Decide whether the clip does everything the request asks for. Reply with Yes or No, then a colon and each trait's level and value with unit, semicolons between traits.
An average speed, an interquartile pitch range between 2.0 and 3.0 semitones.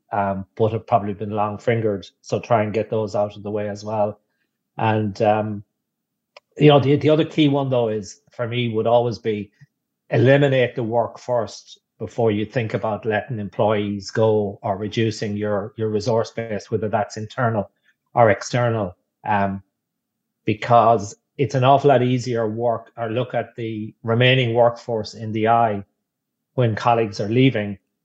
Yes: average, 165 wpm; narrow, 2.5 semitones